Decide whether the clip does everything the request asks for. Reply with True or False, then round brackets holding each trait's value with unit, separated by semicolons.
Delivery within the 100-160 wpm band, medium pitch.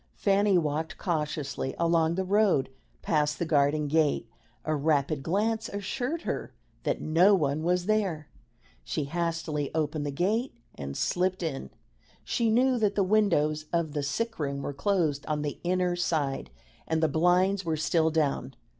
True (155 wpm; 160 Hz)